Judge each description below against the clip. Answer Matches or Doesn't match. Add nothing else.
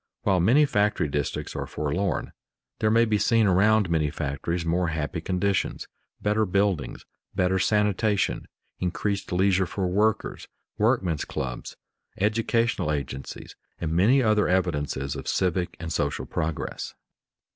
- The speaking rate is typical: Doesn't match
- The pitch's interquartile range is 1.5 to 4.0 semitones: Doesn't match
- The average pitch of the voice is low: Matches